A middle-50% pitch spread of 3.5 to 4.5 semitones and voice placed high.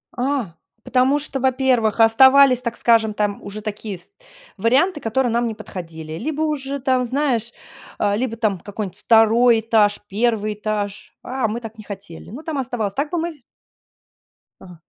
Yes: average, 3.9 semitones; high, 230 Hz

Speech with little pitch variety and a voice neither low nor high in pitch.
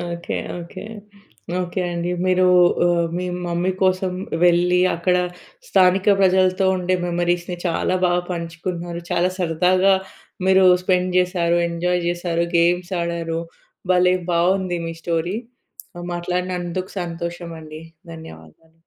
Yes: narrow, 1.3 semitones; medium, 175 Hz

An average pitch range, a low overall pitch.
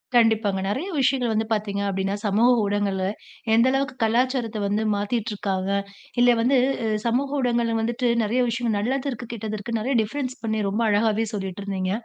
No: average, 3.2 semitones; high, 225 Hz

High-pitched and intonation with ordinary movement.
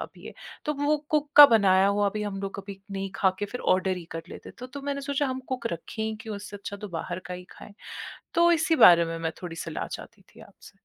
No: high, 200 Hz; wide, 5.8 semitones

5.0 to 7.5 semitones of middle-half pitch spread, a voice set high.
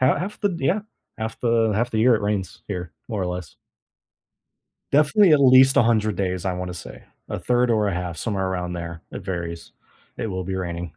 No: wide, 5.4 semitones; low, 100 Hz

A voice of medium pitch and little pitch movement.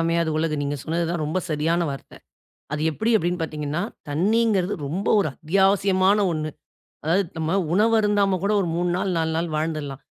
No: medium, 170 Hz; average, 3.9 semitones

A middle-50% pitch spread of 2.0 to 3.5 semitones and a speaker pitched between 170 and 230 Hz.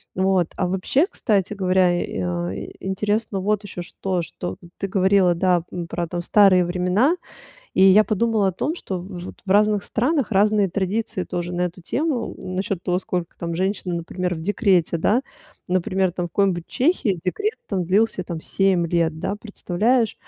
Yes: average, 2.9 semitones; high, 190 Hz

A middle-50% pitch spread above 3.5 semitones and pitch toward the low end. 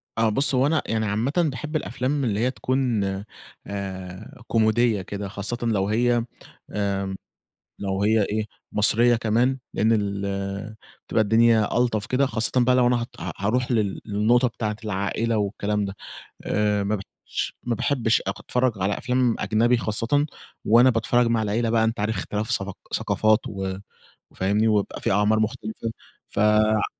No: average, 2.7 semitones; low, 110 Hz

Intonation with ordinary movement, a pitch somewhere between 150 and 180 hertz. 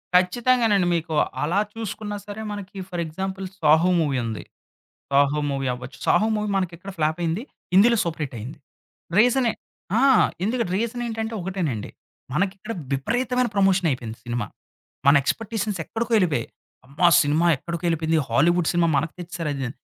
No: wide, 5.8 semitones; medium, 175 Hz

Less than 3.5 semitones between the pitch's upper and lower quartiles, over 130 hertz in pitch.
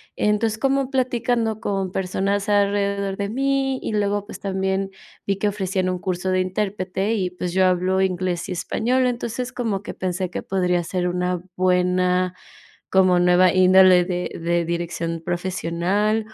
Yes: narrow, 2.4 semitones; high, 190 Hz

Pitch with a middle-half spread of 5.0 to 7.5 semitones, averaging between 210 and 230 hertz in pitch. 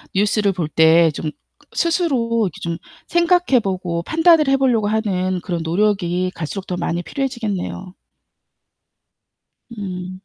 No: wide, 5.6 semitones; high, 195 Hz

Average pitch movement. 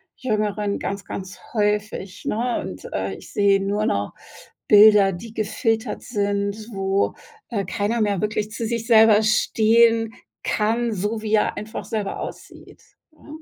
No: narrow, 1.8 semitones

